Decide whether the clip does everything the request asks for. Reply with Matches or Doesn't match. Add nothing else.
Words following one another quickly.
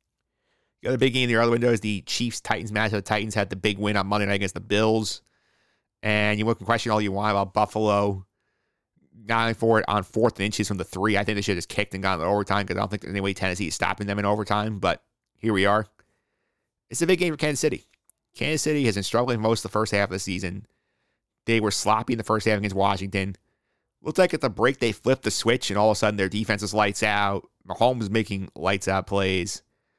Matches